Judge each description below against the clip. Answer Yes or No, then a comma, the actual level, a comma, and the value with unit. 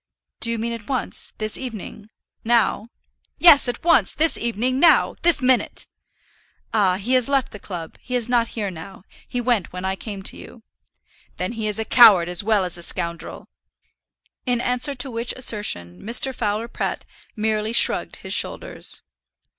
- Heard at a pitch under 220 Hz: No, high, 225 Hz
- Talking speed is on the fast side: No, average, 170 wpm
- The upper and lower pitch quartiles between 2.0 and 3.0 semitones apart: No, average, 3.7 semitones